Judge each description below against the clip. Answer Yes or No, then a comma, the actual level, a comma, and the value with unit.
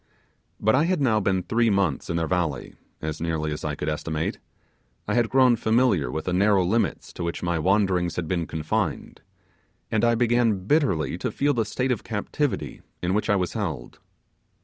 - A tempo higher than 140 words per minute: Yes, average, 190 wpm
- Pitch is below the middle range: Yes, very low, 95 Hz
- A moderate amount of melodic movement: No, wide, 5.9 semitones